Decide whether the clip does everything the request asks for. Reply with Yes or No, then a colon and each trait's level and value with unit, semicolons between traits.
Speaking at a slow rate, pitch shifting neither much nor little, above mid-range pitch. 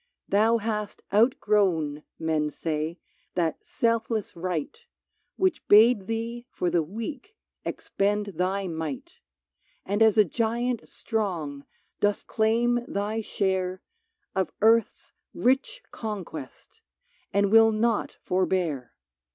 Yes: slow, 110 wpm; average, 4.0 semitones; high, 205 Hz